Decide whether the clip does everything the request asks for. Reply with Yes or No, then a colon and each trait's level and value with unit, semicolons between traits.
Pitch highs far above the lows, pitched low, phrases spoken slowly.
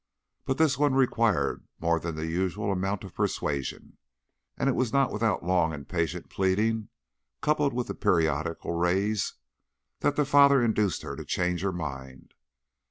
No: wide, 6.3 semitones; very low, 95 Hz; average, 160 wpm